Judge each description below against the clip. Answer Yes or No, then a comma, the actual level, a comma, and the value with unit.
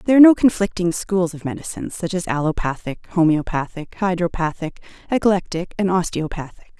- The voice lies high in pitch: No, medium, 180 Hz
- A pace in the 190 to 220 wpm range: No, slow, 135 wpm